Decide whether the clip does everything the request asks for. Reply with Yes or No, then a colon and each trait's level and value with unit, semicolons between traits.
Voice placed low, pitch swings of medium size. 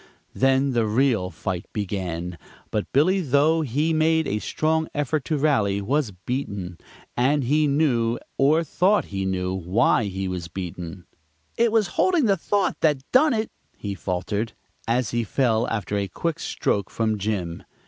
No: low, 120 Hz; wide, 7.8 semitones